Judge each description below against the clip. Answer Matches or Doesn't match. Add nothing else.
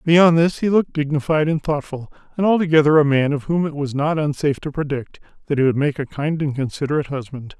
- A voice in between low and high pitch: Matches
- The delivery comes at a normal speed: Doesn't match